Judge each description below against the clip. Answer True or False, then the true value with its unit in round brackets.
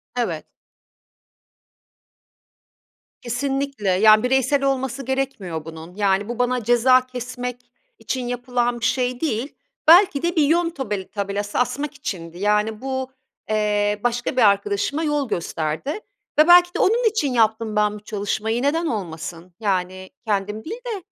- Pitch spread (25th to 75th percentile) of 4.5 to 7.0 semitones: True (4.8 semitones)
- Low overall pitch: False (240 Hz)